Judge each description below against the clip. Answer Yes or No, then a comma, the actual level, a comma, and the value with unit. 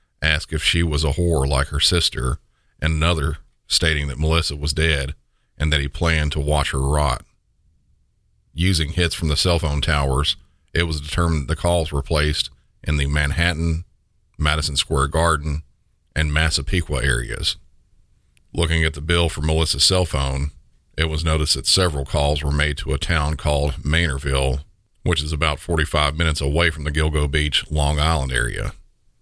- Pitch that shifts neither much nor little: No, narrow, 2.3 semitones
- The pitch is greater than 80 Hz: No, very low, 75 Hz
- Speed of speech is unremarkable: Yes, average, 170 wpm